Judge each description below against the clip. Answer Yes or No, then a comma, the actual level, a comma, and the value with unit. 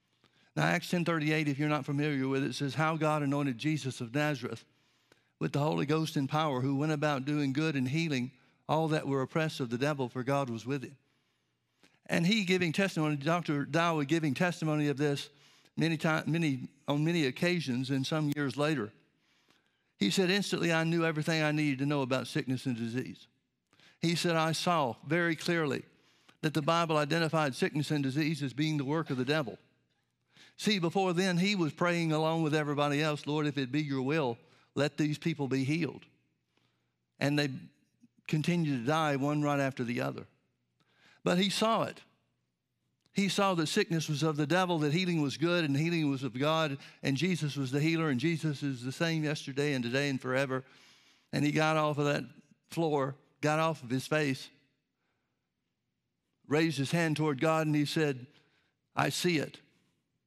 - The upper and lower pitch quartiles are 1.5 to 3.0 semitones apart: Yes, average, 2.7 semitones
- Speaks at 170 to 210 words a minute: Yes, average, 185 wpm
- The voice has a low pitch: No, medium, 150 Hz